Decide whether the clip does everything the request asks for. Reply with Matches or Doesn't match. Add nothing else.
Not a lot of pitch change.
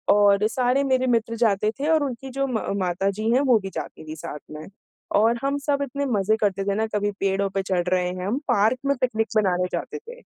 Doesn't match